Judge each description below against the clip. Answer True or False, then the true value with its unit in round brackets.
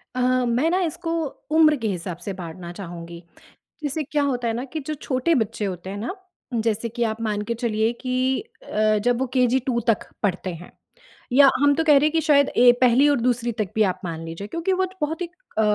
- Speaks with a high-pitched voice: True (240 Hz)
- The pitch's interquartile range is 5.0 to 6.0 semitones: True (5.5 semitones)